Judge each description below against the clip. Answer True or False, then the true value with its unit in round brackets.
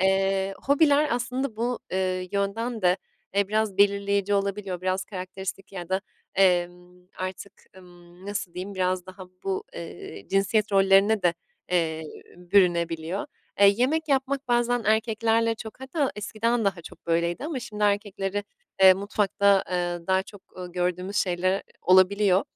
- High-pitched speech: True (195 Hz)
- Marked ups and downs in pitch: False (2.9 semitones)